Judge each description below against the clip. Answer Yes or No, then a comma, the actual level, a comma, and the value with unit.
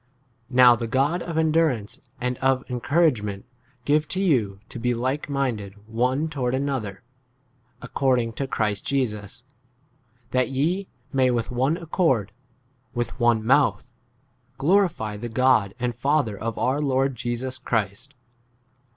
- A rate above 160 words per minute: No, average, 140 wpm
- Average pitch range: Yes, average, 3.6 semitones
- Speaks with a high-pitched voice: No, low, 130 Hz